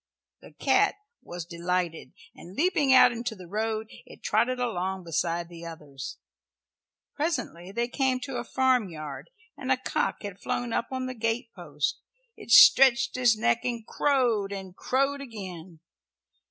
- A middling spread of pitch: No, wide, 6.1 semitones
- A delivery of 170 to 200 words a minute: No, average, 150 wpm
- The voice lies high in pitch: Yes, high, 225 Hz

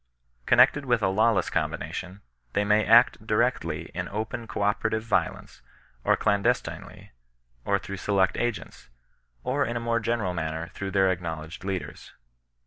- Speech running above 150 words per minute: No, average, 145 wpm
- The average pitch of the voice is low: Yes, low, 105 Hz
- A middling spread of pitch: Yes, average, 3.5 semitones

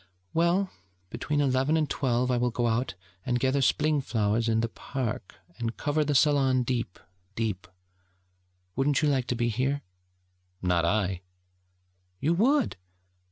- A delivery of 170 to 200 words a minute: No, average, 145 wpm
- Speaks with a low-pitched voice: Yes, low, 130 Hz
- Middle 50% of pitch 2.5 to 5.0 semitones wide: Yes, average, 4.0 semitones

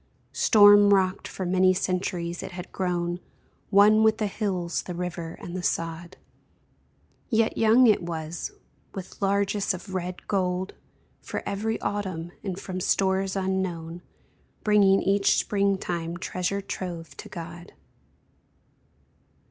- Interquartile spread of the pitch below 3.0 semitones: Yes, narrow, 2.4 semitones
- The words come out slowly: Yes, slow, 125 wpm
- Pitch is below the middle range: No, medium, 185 Hz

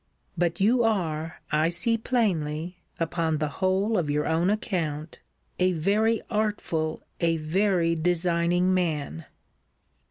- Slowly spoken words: Yes, slow, 120 wpm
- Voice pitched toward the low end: No, medium, 175 Hz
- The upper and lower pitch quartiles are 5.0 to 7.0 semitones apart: No, average, 3.8 semitones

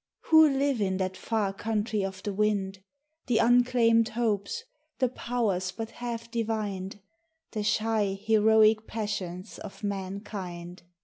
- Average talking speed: No, slow, 125 wpm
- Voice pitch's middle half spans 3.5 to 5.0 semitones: No, average, 2.9 semitones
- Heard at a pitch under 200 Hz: No, high, 215 Hz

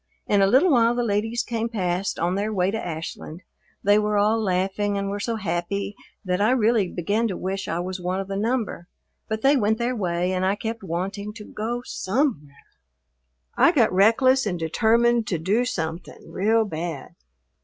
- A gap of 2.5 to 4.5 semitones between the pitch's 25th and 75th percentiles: Yes, average, 3.8 semitones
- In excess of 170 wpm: Yes, average, 185 wpm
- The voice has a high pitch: Yes, high, 205 Hz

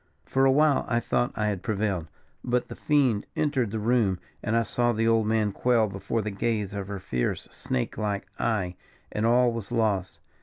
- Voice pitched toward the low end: Yes, low, 110 Hz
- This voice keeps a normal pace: Yes, average, 195 wpm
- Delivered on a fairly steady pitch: No, average, 3.0 semitones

